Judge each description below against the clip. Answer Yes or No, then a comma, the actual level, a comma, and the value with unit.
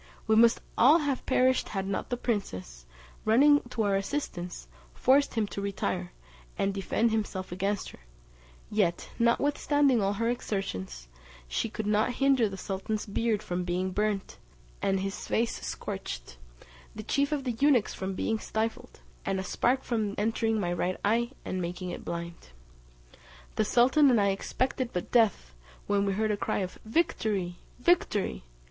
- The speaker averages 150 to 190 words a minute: Yes, average, 160 wpm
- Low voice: No, high, 210 Hz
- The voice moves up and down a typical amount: Yes, average, 4.0 semitones